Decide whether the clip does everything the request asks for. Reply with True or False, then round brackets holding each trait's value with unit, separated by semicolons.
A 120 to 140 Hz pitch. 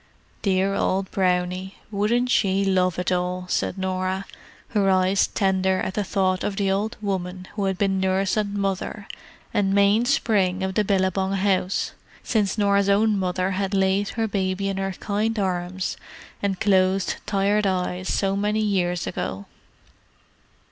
False (195 Hz)